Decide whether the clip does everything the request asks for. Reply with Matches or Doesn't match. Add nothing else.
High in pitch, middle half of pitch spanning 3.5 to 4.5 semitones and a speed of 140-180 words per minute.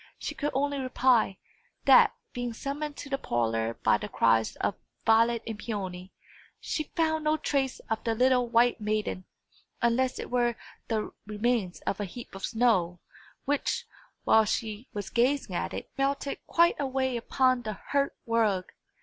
Matches